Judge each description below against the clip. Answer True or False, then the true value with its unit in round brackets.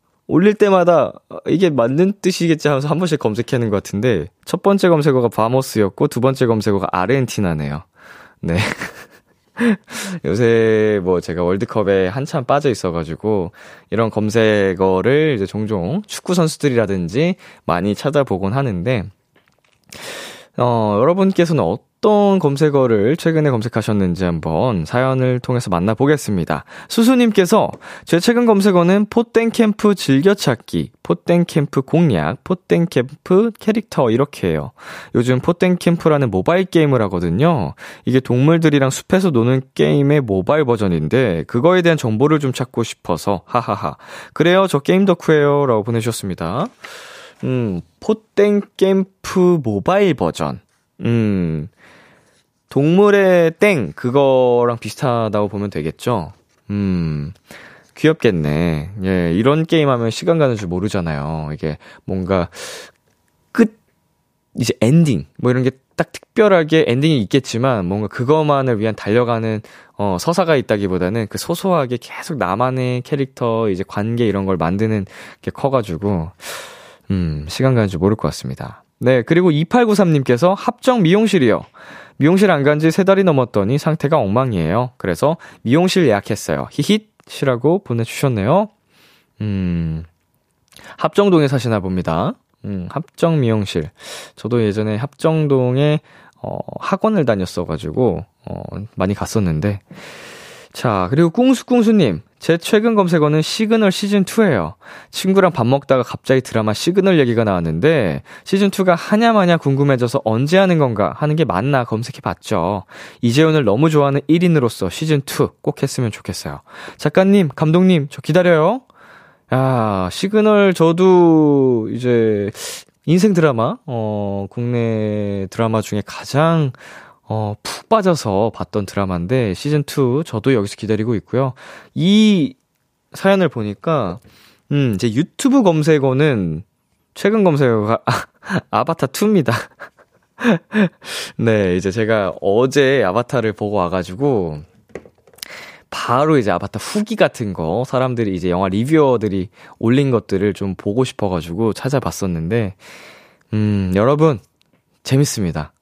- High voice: False (130 Hz)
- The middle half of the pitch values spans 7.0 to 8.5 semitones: True (8.2 semitones)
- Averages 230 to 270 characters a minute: False (290 characters per minute)